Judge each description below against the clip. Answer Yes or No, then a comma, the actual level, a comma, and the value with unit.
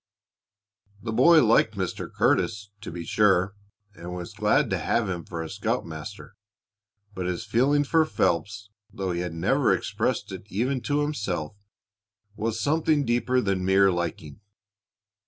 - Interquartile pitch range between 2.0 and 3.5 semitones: No, average, 5.2 semitones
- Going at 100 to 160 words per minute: Yes, average, 145 wpm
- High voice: No, low, 100 Hz